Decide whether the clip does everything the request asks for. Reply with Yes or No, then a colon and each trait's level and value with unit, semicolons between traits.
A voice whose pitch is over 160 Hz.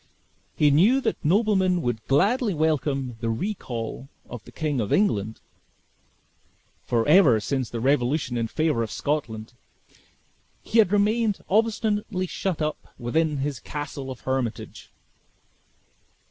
No: medium, 145 Hz